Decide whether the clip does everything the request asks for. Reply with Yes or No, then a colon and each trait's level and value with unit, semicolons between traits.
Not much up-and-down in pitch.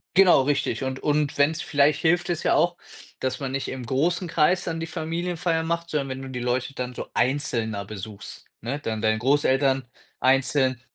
No: average, 4.1 semitones